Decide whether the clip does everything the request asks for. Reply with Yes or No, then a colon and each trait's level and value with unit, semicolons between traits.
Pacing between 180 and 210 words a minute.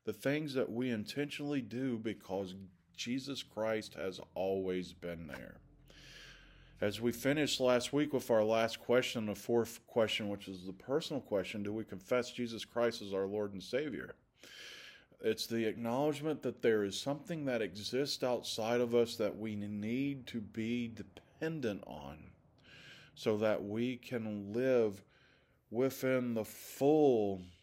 No: average, 145 wpm